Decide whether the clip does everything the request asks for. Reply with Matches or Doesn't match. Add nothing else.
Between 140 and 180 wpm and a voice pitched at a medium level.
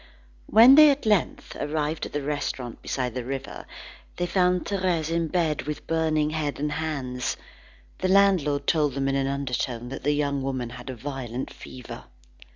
Matches